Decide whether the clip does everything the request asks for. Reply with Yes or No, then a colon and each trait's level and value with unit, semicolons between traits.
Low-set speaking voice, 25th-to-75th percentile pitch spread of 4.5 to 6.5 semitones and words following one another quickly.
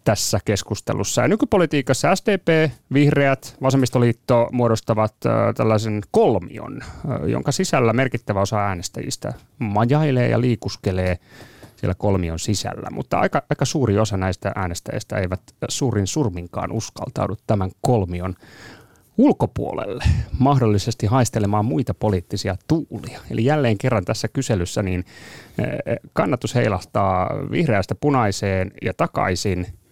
No: low, 115 Hz; average, 4.9 semitones; average, 105 wpm